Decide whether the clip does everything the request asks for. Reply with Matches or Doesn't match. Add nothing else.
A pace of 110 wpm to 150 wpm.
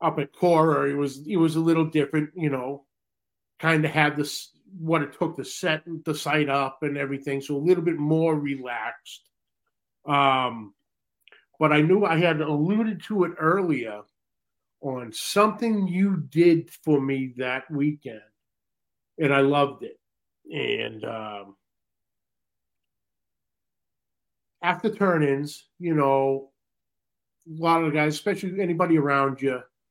Matches